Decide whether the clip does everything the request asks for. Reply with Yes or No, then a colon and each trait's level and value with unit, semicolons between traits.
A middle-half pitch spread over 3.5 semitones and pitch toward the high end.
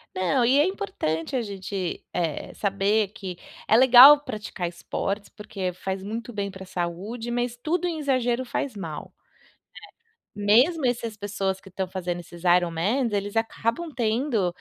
Yes: average, 4.7 semitones; high, 210 Hz